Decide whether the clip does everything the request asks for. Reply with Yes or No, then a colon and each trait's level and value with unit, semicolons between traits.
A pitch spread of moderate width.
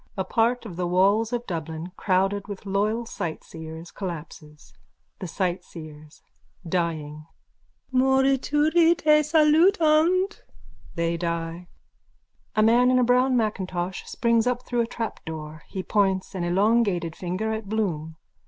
No: wide, 6.3 semitones